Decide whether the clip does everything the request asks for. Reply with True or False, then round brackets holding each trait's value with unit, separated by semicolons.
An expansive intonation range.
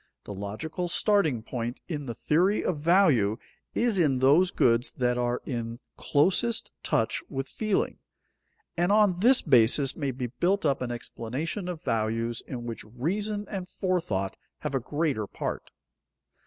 True (7.3 semitones)